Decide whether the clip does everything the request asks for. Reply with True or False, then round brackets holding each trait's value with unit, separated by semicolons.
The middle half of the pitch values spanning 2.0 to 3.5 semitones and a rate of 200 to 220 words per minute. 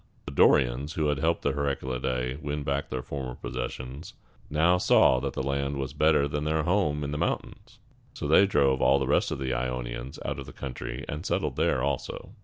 True (2.4 semitones; 205 wpm)